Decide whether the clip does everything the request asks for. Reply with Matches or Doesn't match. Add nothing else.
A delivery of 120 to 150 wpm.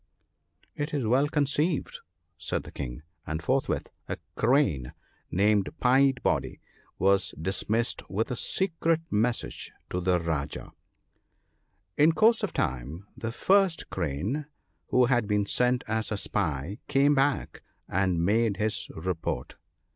Matches